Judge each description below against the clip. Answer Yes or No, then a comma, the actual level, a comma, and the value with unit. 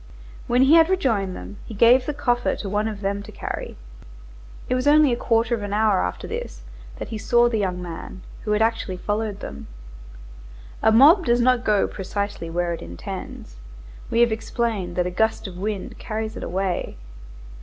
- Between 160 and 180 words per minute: No, average, 190 wpm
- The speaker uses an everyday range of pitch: Yes, average, 4.2 semitones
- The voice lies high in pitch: Yes, high, 215 Hz